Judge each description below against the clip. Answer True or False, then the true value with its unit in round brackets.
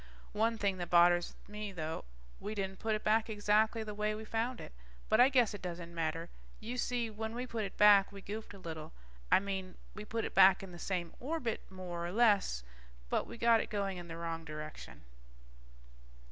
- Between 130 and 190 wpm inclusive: False (205 wpm)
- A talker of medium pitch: False (205 Hz)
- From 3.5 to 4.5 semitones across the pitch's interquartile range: True (3.9 semitones)